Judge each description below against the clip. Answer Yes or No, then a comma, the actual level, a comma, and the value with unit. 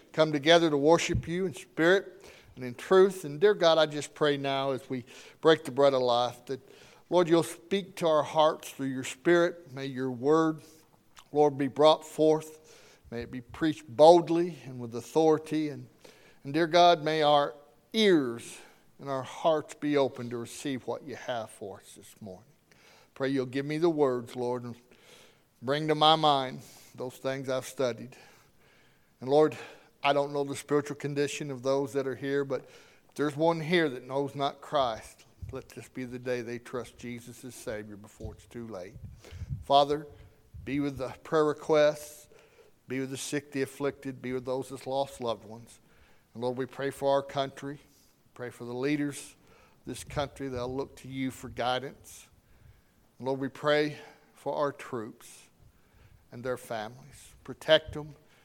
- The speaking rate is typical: Yes, average, 180 wpm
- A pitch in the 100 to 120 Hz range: No, medium, 140 Hz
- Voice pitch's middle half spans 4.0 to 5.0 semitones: No, average, 3.4 semitones